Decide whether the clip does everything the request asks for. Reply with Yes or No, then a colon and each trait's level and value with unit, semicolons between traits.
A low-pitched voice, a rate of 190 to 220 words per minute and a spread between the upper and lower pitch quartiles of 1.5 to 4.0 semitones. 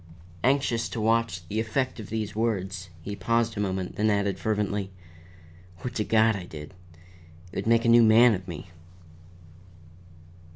No: low, 110 Hz; average, 160 wpm; average, 3.2 semitones